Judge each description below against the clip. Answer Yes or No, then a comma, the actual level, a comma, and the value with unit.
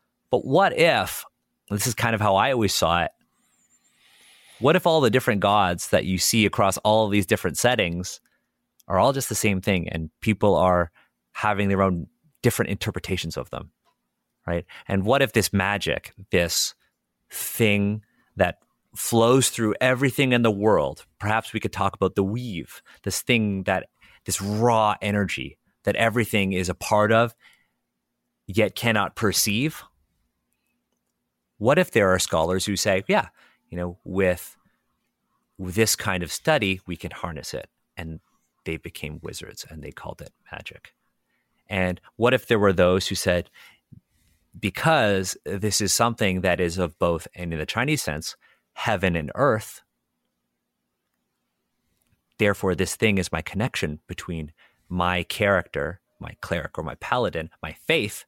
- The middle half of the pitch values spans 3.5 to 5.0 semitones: Yes, average, 3.9 semitones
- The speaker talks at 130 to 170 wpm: Yes, average, 155 wpm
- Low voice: Yes, very low, 95 Hz